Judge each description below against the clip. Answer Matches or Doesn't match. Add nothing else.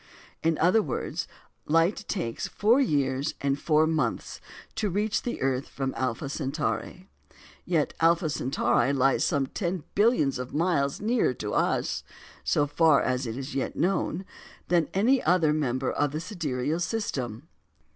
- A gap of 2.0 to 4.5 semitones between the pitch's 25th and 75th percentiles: Doesn't match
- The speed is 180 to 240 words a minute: Doesn't match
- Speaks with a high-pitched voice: Doesn't match